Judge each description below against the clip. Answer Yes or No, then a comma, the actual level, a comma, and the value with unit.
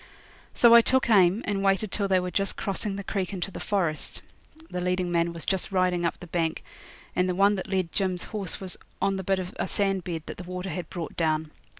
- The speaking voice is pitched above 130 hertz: Yes, medium, 185 Hz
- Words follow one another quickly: Yes, fast, 235 wpm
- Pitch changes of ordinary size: No, narrow, 2.0 semitones